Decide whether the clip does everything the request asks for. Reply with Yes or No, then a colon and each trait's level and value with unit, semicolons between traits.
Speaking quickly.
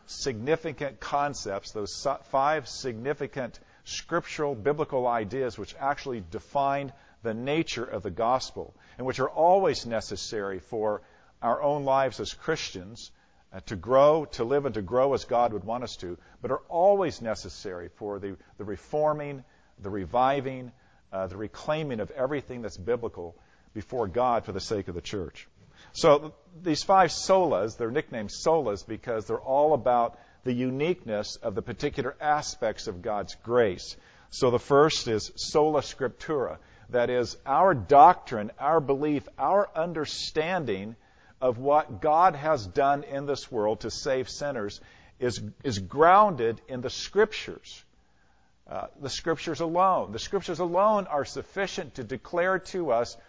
No: average, 145 wpm